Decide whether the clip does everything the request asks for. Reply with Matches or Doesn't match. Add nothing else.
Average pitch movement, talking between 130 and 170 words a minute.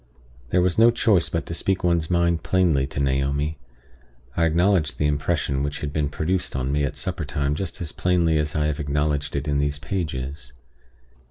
Doesn't match